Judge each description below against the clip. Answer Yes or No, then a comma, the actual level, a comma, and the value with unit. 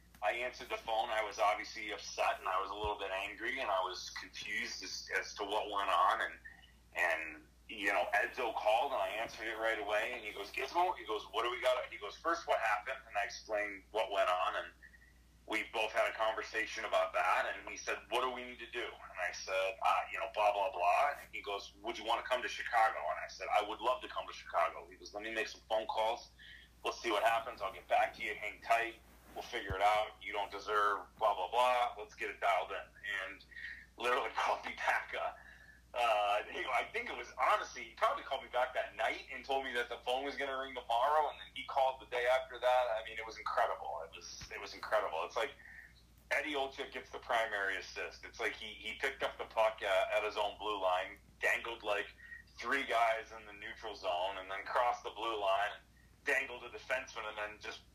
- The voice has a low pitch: Yes, low, 110 Hz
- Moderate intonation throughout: Yes, average, 3.5 semitones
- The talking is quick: Yes, fast, 235 wpm